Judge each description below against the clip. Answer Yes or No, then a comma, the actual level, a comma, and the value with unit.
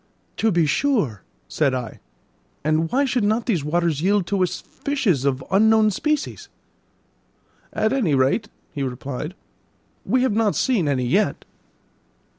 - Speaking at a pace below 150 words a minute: Yes, average, 140 wpm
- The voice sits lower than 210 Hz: Yes, medium, 185 Hz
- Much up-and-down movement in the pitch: Yes, wide, 7.6 semitones